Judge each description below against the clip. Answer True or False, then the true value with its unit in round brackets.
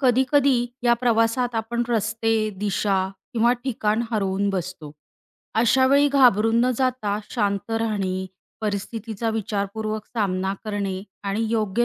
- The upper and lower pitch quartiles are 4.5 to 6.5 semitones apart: False (3.0 semitones)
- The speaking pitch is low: False (220 Hz)